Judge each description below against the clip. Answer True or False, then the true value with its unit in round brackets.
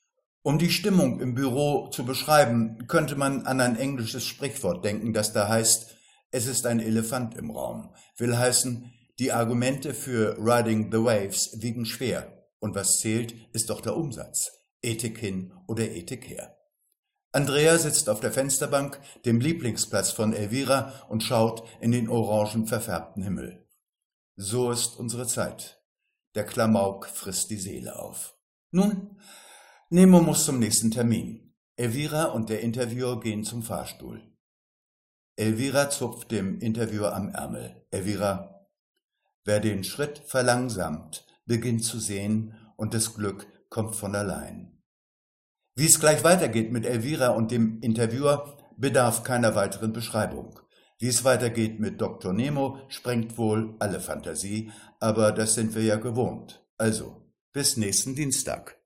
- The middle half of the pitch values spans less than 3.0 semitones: False (3.5 semitones)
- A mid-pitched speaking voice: False (115 Hz)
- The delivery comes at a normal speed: True (140 wpm)